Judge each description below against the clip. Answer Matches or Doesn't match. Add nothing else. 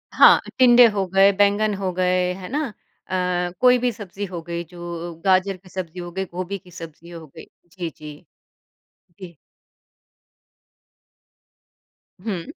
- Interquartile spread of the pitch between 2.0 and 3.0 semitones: Matches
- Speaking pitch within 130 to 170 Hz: Doesn't match